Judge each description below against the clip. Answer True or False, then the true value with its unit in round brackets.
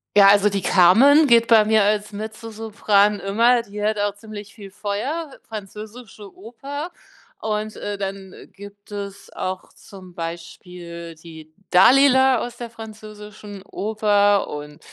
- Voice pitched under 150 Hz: False (205 Hz)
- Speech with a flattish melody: True (2.1 semitones)